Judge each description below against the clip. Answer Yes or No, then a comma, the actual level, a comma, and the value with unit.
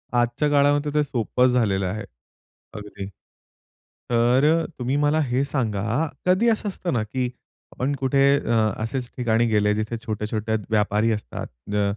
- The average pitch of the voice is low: Yes, low, 120 Hz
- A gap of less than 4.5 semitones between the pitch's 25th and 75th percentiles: No, average, 4.8 semitones